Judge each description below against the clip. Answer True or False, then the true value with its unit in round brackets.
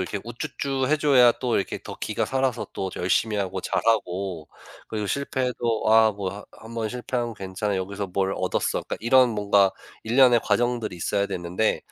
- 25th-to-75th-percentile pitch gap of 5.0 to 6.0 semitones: False (3.9 semitones)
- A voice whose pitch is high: False (110 Hz)